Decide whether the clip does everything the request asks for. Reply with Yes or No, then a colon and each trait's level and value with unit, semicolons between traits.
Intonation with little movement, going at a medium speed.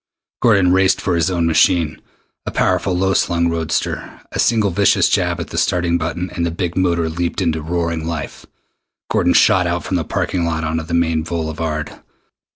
Yes: narrow, 1.9 semitones; average, 180 wpm